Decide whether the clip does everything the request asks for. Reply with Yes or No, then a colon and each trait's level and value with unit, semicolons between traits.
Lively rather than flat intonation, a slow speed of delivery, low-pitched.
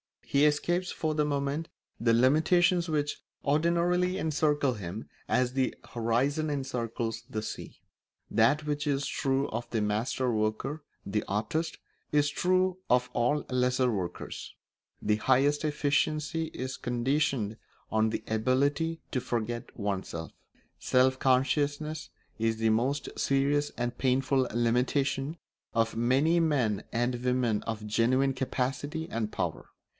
No: average, 4.1 semitones; slow, 125 wpm; low, 130 Hz